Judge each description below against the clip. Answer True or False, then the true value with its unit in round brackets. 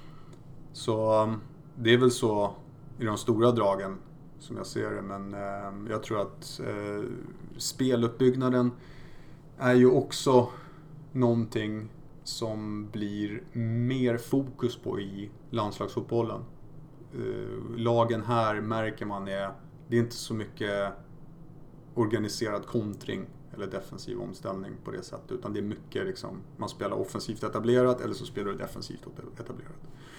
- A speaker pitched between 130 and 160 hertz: False (120 Hz)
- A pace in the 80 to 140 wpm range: True (125 wpm)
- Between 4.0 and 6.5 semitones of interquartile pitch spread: True (4.6 semitones)